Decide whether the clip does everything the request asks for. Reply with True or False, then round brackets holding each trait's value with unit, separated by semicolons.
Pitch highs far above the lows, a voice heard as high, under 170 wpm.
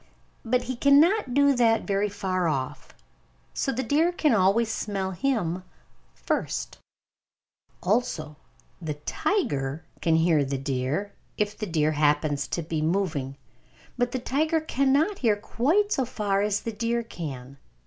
True (8.4 semitones; 205 Hz; 140 wpm)